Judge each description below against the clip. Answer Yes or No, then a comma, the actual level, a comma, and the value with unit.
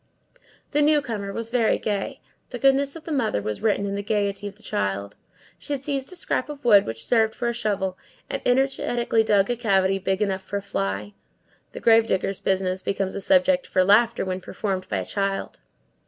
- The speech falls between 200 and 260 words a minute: Yes, fast, 205 wpm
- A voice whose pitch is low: No, high, 205 Hz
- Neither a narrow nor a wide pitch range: Yes, average, 4.2 semitones